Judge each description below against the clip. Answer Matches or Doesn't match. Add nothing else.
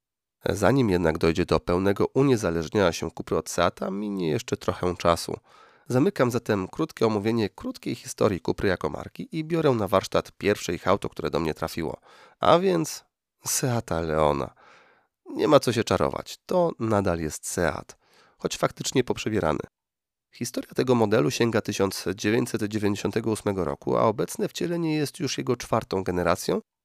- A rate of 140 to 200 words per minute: Matches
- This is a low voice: Matches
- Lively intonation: Matches